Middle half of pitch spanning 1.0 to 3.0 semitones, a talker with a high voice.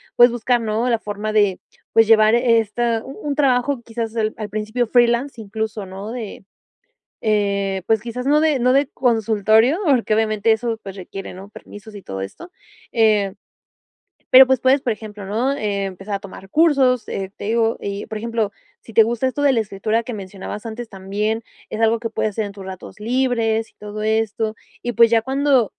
Yes: narrow, 2.6 semitones; high, 225 Hz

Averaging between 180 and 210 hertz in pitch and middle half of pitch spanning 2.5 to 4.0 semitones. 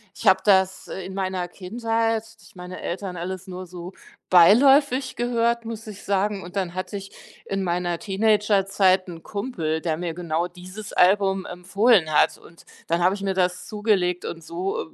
Yes: high, 190 Hz; average, 2.8 semitones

